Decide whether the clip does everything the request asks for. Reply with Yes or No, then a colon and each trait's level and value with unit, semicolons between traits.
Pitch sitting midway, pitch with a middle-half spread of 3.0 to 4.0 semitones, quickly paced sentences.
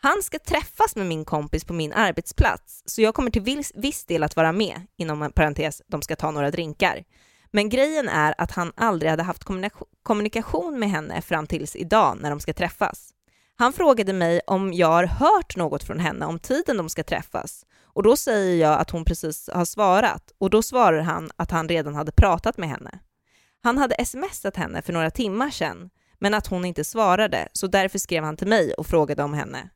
No: medium, 180 Hz; wide, 5.6 semitones; fast, 205 wpm